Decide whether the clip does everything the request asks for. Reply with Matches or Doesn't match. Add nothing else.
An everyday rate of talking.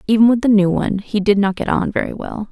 Doesn't match